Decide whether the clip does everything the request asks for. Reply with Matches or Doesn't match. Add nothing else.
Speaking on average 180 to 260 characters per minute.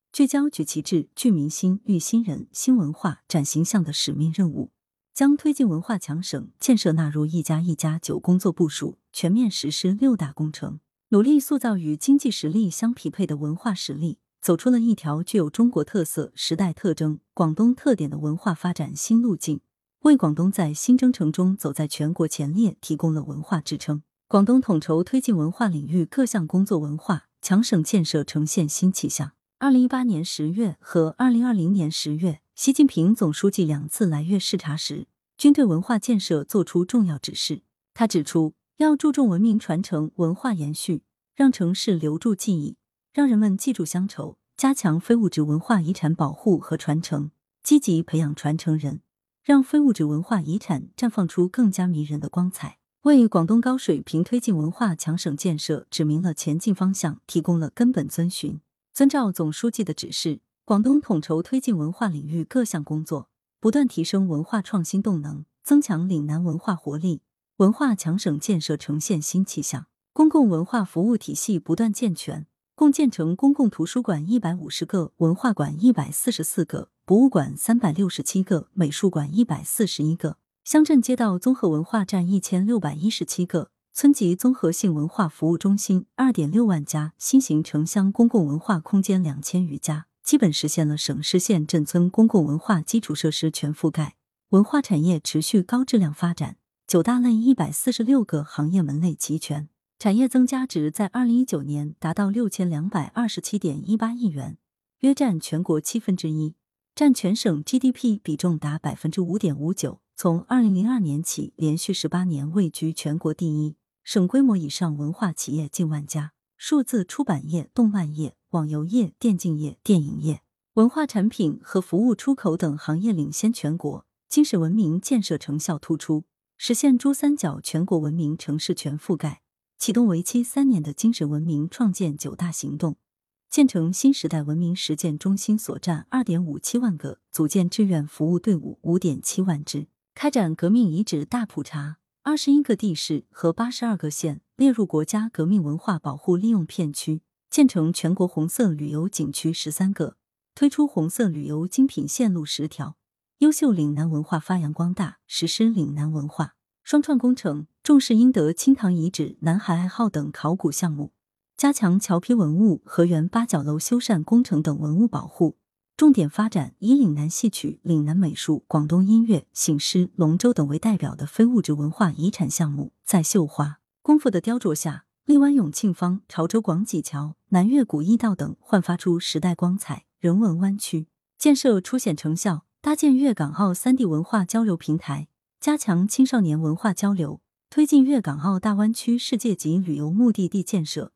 Doesn't match